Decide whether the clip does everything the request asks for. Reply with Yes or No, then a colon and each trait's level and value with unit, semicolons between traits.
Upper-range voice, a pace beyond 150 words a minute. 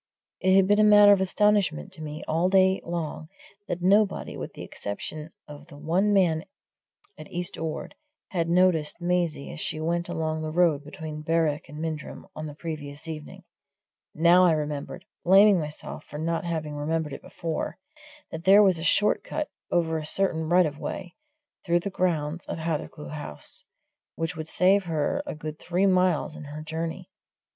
No: medium, 165 Hz; average, 175 wpm